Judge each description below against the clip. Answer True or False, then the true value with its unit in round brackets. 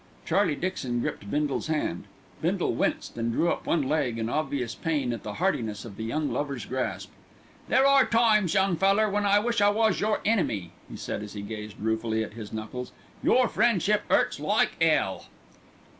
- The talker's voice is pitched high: False (145 Hz)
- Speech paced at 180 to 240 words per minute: True (185 wpm)